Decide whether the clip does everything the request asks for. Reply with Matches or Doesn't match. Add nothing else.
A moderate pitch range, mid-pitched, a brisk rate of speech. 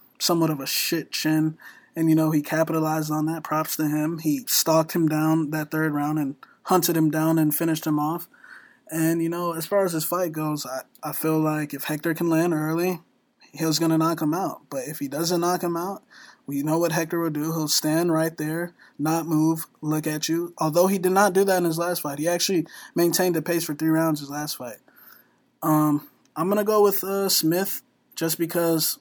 Doesn't match